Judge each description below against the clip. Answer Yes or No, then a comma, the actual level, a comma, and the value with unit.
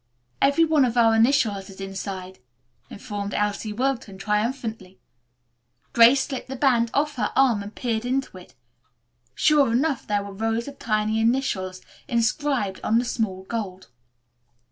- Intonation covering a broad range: No, average, 4.6 semitones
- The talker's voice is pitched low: No, high, 225 Hz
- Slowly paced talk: No, average, 145 wpm